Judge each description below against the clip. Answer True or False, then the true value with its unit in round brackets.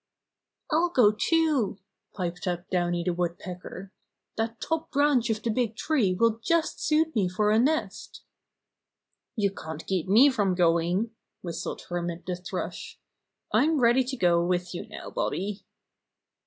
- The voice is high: True (205 Hz)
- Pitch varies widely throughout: True (6.2 semitones)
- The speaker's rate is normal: True (150 wpm)